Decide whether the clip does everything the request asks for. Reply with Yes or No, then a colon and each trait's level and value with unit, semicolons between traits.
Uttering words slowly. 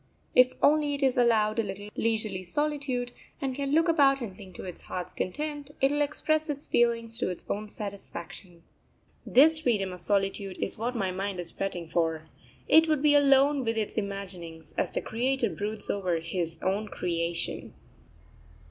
No: average, 175 wpm